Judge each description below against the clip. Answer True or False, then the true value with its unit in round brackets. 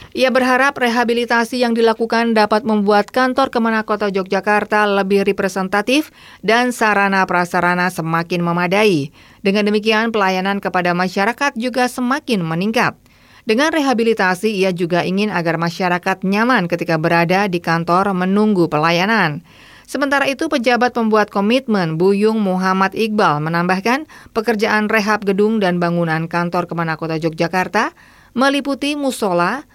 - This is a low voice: False (205 Hz)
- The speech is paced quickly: False (120 wpm)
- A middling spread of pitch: True (4.5 semitones)